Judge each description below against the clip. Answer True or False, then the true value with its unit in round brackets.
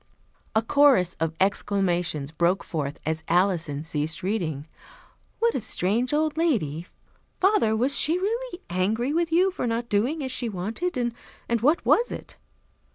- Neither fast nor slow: True (150 wpm)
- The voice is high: True (220 Hz)